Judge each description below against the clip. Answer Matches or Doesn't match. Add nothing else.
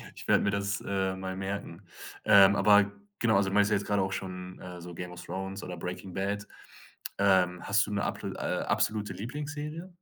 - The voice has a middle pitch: Doesn't match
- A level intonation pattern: Matches